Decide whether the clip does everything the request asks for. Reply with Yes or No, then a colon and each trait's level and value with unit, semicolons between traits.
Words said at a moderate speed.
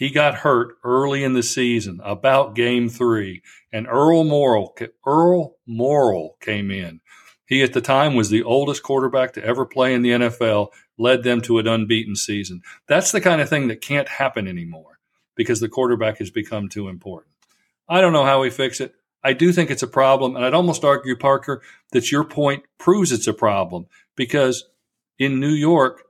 Yes: average, 190 wpm